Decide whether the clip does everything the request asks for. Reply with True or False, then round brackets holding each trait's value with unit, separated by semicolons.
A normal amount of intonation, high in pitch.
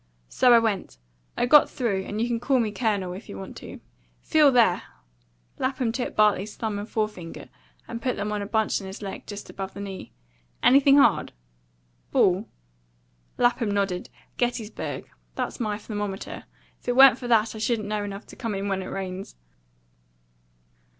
True (3.4 semitones; 215 Hz)